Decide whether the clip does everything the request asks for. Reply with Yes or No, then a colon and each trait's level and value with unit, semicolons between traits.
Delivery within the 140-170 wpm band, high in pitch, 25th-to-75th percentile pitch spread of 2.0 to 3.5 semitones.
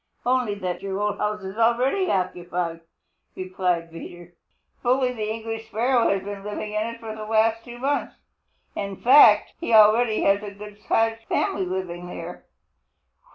Yes: average, 155 wpm; high, 210 Hz; average, 3.1 semitones